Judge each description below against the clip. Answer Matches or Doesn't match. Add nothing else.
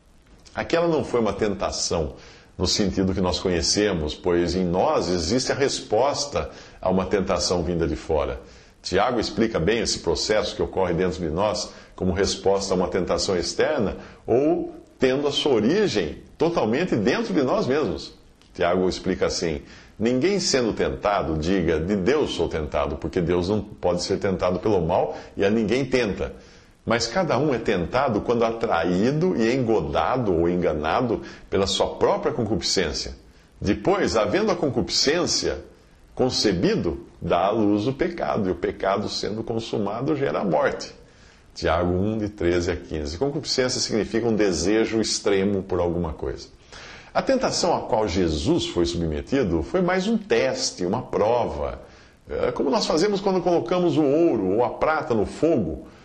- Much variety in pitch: Matches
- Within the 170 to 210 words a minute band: Doesn't match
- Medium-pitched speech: Doesn't match